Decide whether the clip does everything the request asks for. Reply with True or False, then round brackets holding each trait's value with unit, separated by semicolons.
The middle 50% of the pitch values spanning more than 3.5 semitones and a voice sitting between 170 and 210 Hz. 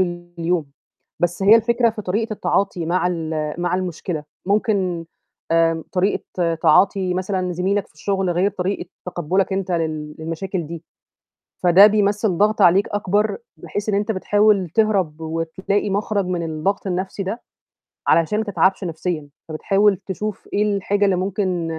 False (3.1 semitones; 185 Hz)